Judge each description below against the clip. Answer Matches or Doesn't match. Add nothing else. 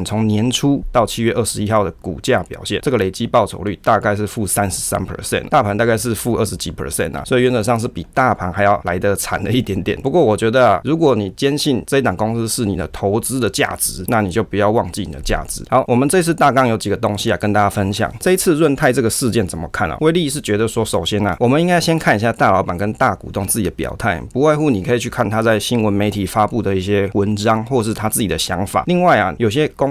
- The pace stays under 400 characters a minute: Doesn't match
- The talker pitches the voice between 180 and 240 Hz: Doesn't match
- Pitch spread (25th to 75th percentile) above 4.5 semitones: Doesn't match